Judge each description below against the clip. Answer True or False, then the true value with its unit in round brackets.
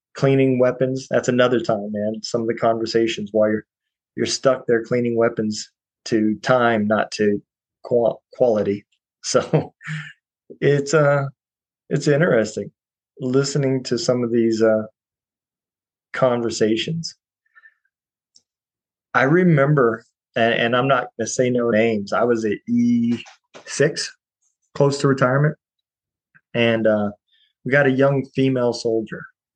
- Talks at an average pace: False (120 wpm)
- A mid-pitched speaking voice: False (120 Hz)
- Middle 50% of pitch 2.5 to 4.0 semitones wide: True (3.4 semitones)